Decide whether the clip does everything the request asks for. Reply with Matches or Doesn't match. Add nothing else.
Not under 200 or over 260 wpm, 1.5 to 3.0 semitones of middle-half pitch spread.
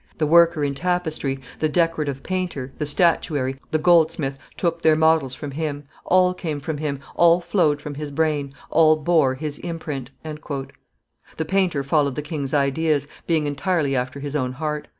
Doesn't match